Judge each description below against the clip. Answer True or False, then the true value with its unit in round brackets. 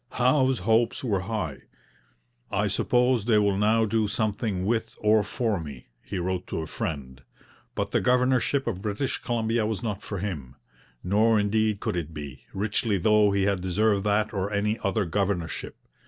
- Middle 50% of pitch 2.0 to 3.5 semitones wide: True (3.0 semitones)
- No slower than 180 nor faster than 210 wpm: False (170 wpm)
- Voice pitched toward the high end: False (105 Hz)